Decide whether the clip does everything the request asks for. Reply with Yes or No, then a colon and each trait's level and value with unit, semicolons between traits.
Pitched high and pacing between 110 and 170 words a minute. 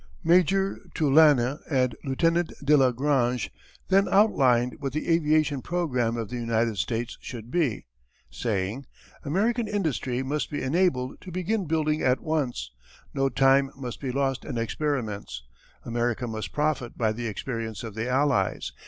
No: low, 135 Hz; average, 145 wpm